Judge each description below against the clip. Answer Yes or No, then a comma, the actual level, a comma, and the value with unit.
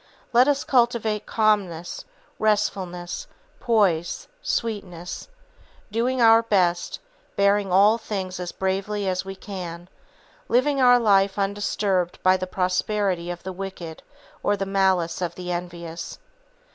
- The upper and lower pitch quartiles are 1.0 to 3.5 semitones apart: Yes, average, 3.0 semitones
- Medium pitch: No, high, 195 Hz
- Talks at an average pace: No, slow, 120 wpm